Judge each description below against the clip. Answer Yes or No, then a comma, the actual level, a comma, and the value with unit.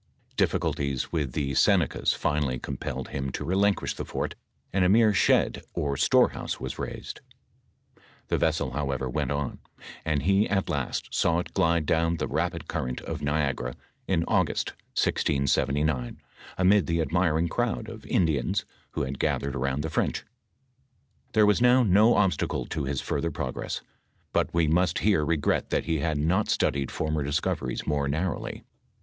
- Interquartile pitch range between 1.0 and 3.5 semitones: No, average, 4.7 semitones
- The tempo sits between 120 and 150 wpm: No, average, 160 wpm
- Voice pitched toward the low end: Yes, very low, 80 Hz